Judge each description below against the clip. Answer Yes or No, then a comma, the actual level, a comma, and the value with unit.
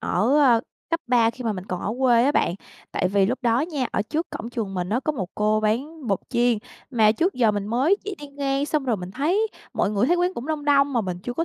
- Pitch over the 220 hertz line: Yes, high, 245 Hz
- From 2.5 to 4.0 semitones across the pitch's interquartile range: No, wide, 5.4 semitones